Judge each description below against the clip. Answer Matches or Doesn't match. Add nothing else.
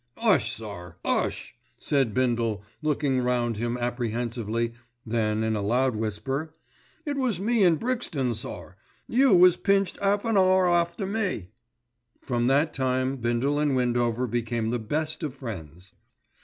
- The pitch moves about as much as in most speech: Doesn't match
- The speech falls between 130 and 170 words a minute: Matches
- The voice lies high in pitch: Doesn't match